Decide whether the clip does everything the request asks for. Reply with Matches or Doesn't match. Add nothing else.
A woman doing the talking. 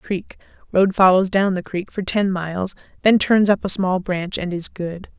Matches